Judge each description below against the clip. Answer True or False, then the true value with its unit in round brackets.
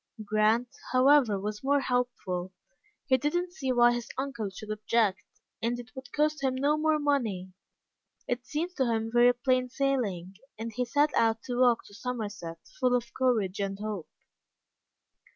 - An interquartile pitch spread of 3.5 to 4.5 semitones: True (3.8 semitones)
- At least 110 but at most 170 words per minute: True (160 wpm)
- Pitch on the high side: True (245 Hz)